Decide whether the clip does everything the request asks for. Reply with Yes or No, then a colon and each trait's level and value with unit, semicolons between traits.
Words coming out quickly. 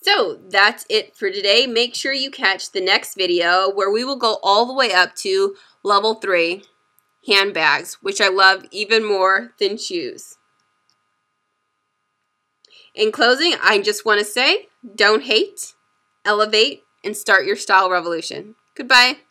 No: average, 145 wpm